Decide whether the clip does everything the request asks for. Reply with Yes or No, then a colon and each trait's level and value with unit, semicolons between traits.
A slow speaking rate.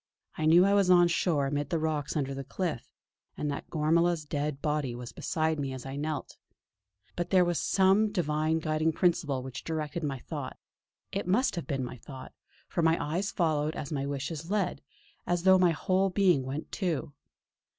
No: average, 185 wpm